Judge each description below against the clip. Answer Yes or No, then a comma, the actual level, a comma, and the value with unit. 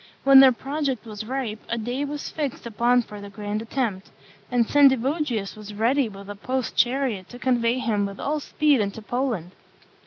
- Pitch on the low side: No, high, 240 Hz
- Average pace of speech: Yes, average, 180 wpm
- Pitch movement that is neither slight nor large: Yes, average, 4.2 semitones